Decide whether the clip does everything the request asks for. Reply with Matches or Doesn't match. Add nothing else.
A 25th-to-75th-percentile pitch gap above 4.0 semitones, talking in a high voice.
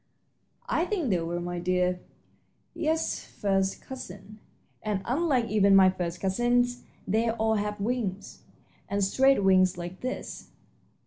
Matches